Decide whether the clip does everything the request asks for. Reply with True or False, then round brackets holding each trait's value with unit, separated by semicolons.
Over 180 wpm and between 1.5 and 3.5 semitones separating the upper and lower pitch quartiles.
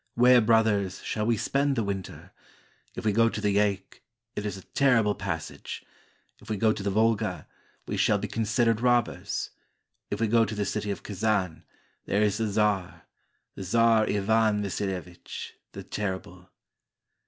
False (165 wpm; 2.4 semitones)